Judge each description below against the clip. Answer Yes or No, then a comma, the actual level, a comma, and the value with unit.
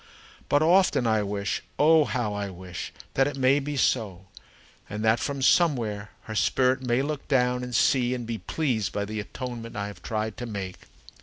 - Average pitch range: Yes, average, 4.3 semitones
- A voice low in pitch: Yes, low, 120 Hz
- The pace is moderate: Yes, average, 185 wpm